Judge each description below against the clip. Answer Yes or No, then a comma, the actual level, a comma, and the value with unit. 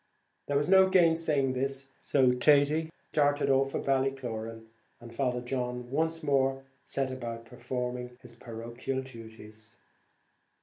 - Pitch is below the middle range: Yes, low, 130 Hz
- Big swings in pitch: No, narrow, 2.6 semitones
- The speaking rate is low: Yes, slow, 125 wpm